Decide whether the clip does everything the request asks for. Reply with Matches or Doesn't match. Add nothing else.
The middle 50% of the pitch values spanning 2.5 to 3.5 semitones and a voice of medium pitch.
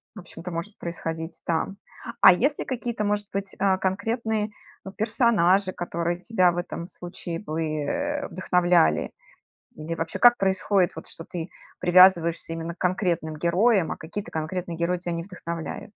Matches